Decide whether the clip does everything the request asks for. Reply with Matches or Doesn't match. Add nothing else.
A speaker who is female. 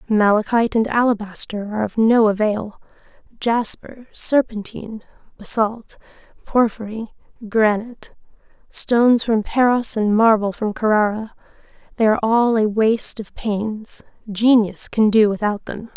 Matches